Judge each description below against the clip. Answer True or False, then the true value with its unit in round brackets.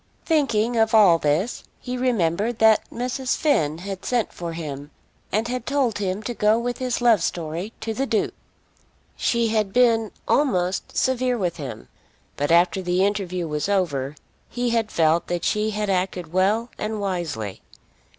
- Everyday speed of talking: True (160 wpm)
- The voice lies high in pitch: True (210 Hz)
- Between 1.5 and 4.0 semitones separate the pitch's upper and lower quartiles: False (5.2 semitones)